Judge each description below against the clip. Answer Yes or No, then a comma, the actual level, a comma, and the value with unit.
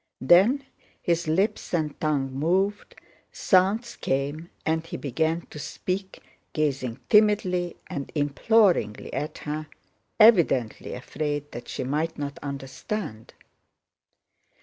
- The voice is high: No, medium, 155 Hz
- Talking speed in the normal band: No, slow, 105 wpm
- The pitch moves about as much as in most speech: Yes, average, 4.8 semitones